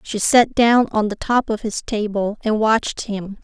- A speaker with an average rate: No, fast, 210 wpm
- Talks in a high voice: Yes, high, 215 Hz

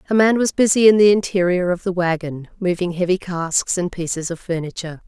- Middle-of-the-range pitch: Yes, medium, 180 Hz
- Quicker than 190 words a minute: Yes, average, 200 wpm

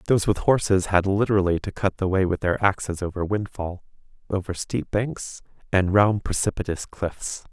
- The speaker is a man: Yes, male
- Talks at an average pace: Yes, average, 170 wpm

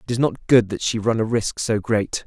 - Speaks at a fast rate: Yes, fast, 290 wpm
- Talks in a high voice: No, low, 110 Hz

